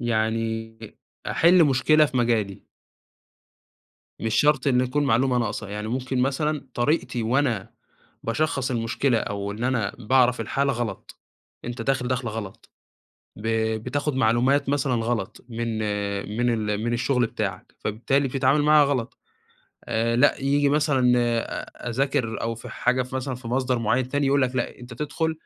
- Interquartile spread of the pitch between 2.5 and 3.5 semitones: Yes, average, 3.2 semitones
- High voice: No, low, 125 Hz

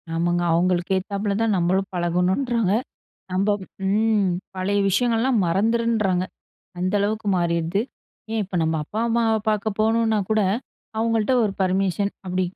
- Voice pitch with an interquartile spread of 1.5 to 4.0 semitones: Yes, average, 3.3 semitones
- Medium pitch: No, high, 200 Hz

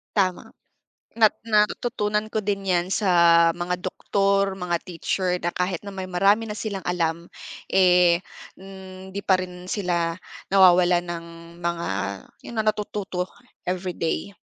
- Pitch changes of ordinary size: No, narrow, 1.9 semitones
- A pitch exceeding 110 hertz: Yes, medium, 185 Hz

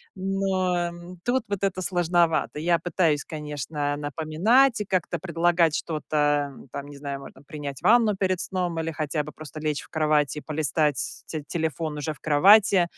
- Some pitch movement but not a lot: Yes, average, 3.7 semitones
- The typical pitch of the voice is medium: Yes, medium, 160 Hz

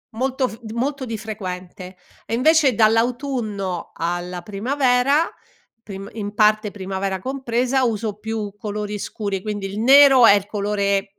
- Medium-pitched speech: No, high, 215 Hz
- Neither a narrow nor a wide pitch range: Yes, average, 3.9 semitones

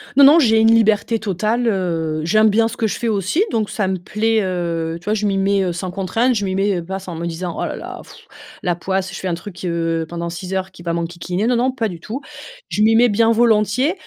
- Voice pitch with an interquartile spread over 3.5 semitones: Yes, average, 4.2 semitones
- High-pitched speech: Yes, high, 195 Hz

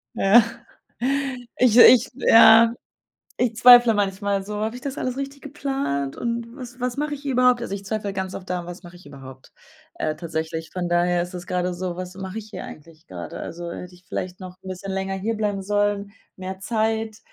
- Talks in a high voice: Yes, high, 195 Hz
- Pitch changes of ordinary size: Yes, average, 4.6 semitones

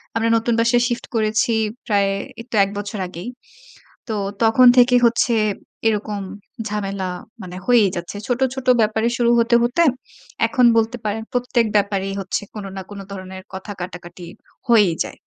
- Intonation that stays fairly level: No, average, 3.2 semitones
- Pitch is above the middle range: Yes, high, 215 Hz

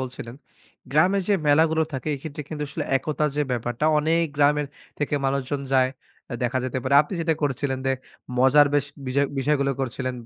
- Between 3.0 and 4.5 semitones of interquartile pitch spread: No, narrow, 2.5 semitones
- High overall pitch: No, medium, 140 Hz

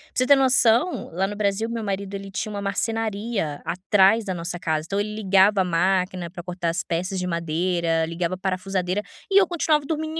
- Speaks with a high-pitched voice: Yes, high, 195 Hz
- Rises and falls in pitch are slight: No, average, 3.5 semitones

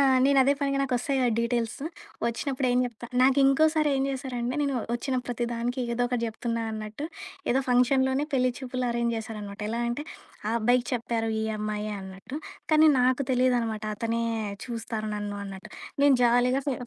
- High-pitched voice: Yes, high, 245 Hz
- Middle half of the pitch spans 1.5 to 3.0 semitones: Yes, narrow, 2.5 semitones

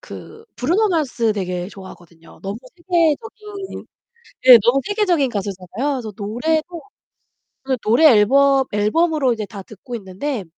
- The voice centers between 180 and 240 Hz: No, very high, 250 Hz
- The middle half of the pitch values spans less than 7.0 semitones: No, wide, 7.8 semitones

